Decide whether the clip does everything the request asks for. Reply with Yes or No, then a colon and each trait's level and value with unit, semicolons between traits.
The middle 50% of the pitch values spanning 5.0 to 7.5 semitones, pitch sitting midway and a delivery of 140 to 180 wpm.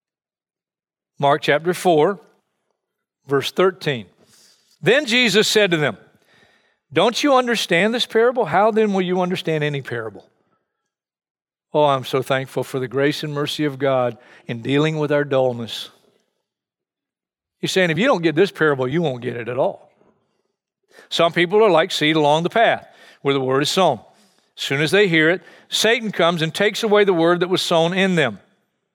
Yes: wide, 5.6 semitones; medium, 160 Hz; average, 170 wpm